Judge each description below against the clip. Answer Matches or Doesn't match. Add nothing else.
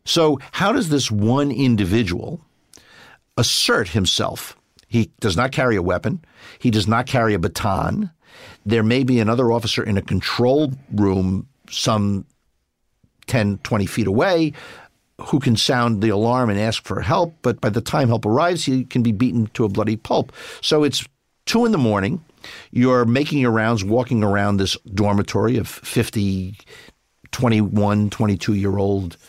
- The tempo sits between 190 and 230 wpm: Doesn't match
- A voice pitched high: Doesn't match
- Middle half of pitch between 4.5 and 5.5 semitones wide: Doesn't match